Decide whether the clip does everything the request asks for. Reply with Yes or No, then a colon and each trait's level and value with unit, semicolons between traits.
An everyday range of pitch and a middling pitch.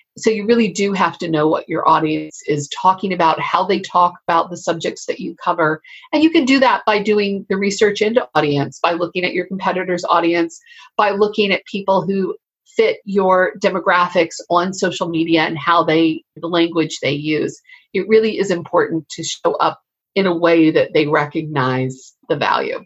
Yes: average, 4.3 semitones; medium, 180 Hz